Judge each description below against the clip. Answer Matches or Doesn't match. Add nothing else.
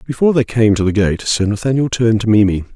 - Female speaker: Doesn't match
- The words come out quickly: Matches